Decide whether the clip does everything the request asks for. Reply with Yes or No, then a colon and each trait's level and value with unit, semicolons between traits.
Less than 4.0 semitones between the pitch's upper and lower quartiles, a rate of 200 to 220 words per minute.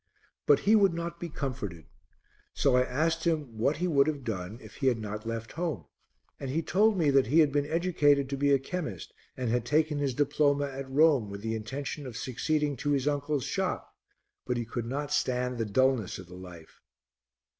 No: average, 4.4 semitones; fast, 205 wpm